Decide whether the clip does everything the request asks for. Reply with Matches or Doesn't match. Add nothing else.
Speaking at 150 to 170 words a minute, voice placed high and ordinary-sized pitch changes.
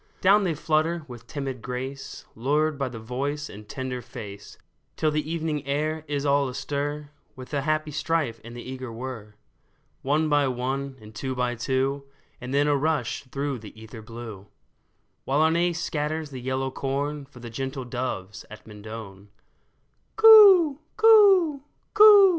Doesn't match